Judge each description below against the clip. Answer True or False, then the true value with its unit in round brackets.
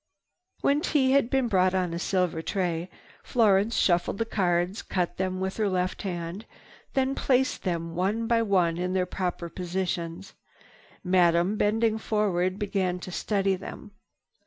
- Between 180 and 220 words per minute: False (155 wpm)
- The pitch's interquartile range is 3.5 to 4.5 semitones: False (3.1 semitones)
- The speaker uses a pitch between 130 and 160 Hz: False (190 Hz)